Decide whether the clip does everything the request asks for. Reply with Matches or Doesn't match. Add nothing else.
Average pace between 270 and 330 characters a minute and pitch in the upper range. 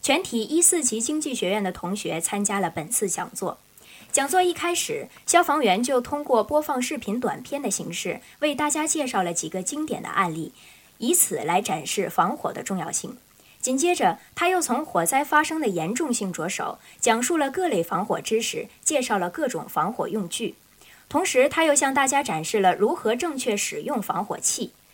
Matches